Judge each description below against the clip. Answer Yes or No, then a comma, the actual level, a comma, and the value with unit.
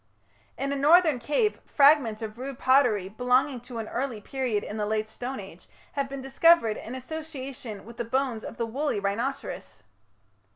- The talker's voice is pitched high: Yes, very high, 255 Hz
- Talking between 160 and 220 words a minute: Yes, average, 170 wpm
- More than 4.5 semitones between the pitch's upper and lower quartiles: No, average, 3.9 semitones